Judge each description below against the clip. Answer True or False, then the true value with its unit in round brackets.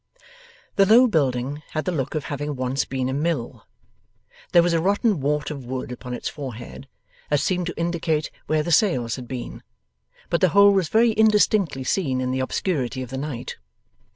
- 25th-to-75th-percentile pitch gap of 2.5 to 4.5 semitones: False (5.4 semitones)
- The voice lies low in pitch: False (150 Hz)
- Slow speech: False (185 wpm)